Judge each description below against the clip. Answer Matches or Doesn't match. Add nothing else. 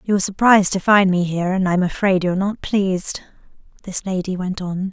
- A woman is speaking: Matches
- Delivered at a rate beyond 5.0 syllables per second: Matches